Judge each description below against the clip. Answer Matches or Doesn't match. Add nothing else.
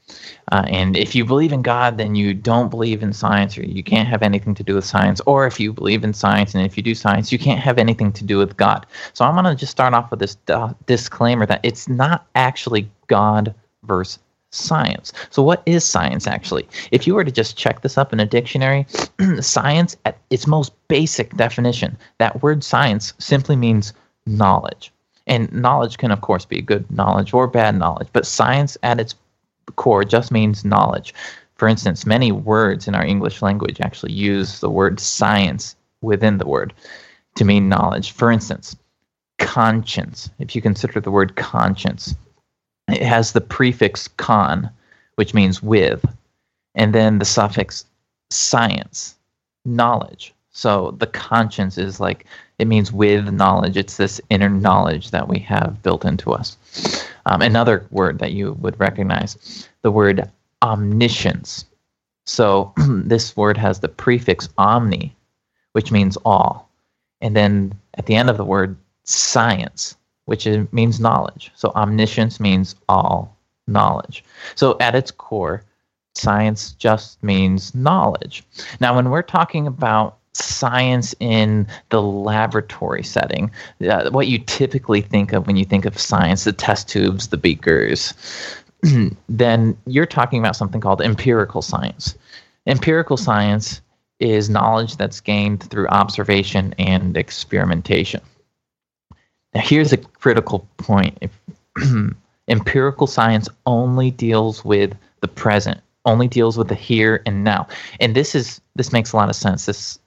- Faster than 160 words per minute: Doesn't match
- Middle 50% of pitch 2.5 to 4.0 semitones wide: Matches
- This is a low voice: Matches